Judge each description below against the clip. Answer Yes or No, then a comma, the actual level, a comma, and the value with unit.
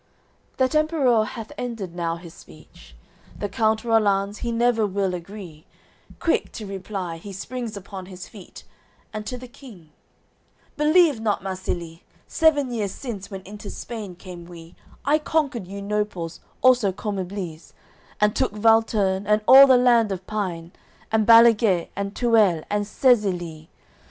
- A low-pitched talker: No, high, 210 Hz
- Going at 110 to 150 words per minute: Yes, average, 145 wpm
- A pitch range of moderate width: Yes, average, 4.1 semitones